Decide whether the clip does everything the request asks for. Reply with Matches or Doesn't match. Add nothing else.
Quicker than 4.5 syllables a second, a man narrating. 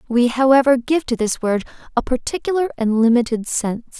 Doesn't match